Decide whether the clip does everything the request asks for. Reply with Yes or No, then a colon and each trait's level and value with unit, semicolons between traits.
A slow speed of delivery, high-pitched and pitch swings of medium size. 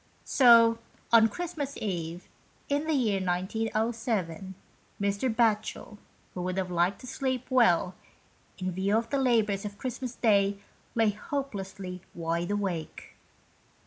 Yes: slow, 125 wpm; high, 210 Hz; average, 4.2 semitones